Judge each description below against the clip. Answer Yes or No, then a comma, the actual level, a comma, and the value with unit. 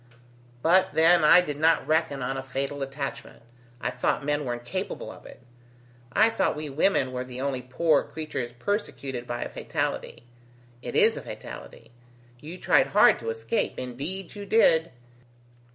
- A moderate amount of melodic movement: Yes, average, 4.3 semitones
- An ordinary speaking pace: Yes, average, 160 wpm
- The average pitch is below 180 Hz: Yes, medium, 140 Hz